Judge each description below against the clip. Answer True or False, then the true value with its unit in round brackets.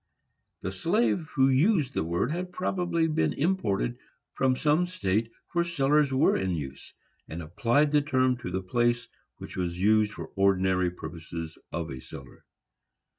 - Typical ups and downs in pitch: False (8.8 semitones)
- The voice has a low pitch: True (120 Hz)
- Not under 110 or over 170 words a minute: True (160 wpm)